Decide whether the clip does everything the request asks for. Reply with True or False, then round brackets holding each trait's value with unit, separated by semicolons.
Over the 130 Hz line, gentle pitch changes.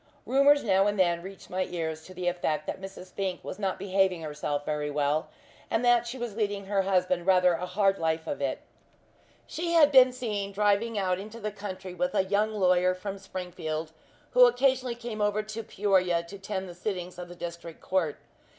False (190 Hz; 3.1 semitones)